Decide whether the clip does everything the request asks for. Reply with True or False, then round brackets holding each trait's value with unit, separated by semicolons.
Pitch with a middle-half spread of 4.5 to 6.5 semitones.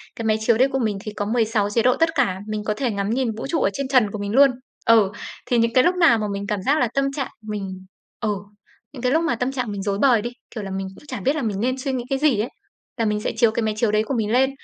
False (3.8 semitones)